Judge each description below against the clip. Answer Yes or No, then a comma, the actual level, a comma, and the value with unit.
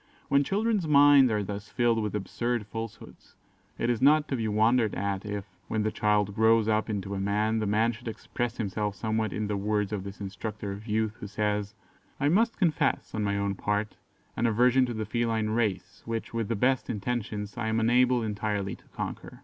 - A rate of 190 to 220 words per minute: Yes, average, 200 wpm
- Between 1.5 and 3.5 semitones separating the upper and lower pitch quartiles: Yes, narrow, 2.5 semitones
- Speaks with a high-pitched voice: No, low, 110 Hz